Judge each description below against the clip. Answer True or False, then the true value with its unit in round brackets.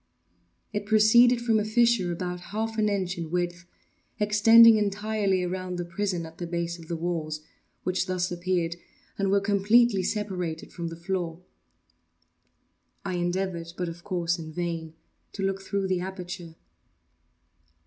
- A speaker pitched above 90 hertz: True (185 Hz)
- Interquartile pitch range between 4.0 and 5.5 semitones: False (3.1 semitones)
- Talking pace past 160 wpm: False (150 wpm)